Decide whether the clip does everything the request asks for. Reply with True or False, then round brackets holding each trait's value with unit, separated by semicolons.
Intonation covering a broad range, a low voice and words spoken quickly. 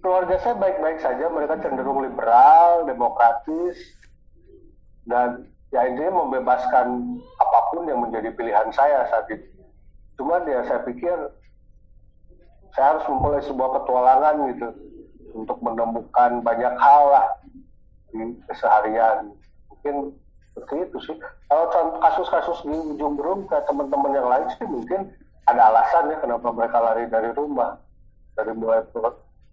False (6.7 semitones; 130 Hz; 125 wpm)